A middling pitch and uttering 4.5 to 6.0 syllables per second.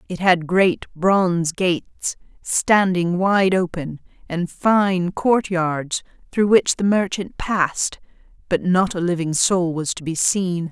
No: medium, 180 Hz; 3.6 syllables/s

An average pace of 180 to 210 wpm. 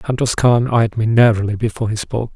Yes: fast, 205 wpm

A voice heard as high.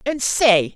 Yes: high, 225 Hz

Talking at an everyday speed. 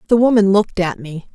No: fast, 225 wpm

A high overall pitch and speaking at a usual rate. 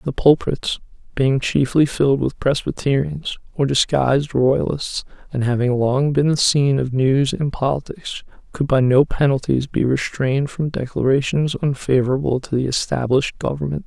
No: low, 135 Hz; average, 145 wpm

